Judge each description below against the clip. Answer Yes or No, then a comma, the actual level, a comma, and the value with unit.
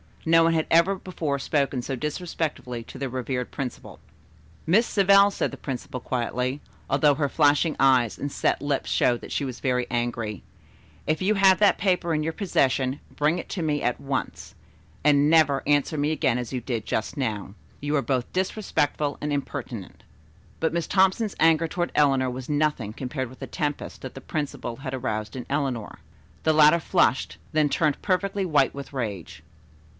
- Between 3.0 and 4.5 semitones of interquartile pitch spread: Yes, average, 4.1 semitones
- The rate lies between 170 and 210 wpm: Yes, average, 180 wpm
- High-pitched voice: No, medium, 145 Hz